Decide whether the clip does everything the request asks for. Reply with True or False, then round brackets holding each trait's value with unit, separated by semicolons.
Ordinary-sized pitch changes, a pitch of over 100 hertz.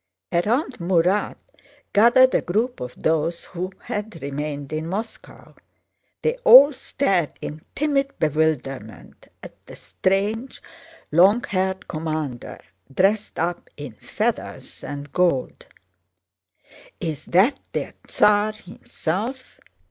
False (6.0 semitones; 185 Hz)